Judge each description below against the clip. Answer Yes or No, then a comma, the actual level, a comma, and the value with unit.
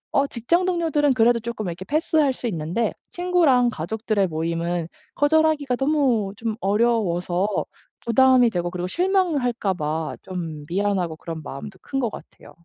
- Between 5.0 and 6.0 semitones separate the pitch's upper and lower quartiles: No, wide, 7.7 semitones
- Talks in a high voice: Yes, high, 225 Hz